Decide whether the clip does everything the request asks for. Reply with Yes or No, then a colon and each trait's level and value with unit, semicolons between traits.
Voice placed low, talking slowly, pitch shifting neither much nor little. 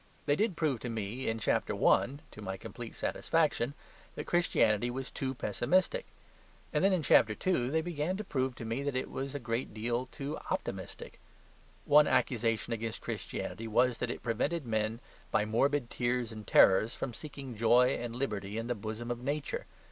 No: low, 120 Hz; average, 180 wpm; average, 4.0 semitones